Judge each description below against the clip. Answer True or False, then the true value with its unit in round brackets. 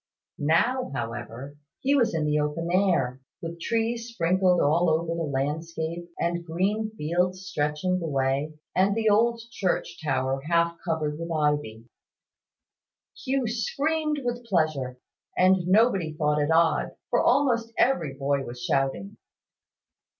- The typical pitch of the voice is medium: True (170 Hz)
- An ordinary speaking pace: False (130 wpm)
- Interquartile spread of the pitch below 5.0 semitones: False (5.3 semitones)